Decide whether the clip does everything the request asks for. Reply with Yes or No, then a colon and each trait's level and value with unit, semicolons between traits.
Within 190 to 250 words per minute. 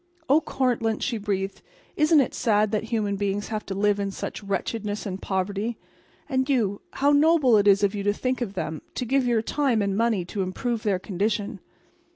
Yes: average, 195 wpm